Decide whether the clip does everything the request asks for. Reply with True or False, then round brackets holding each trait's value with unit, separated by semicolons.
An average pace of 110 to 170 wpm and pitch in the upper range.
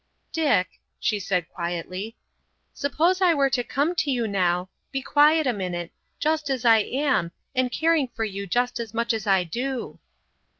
True (160 wpm; 240 Hz)